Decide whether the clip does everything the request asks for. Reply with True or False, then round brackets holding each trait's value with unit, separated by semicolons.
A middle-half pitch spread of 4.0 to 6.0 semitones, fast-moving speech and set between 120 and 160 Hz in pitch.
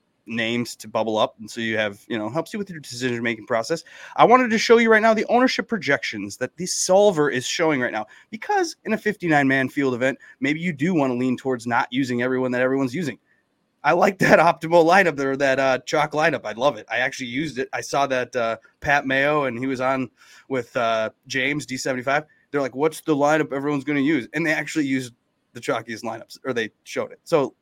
True (4.5 semitones; 230 wpm; 140 Hz)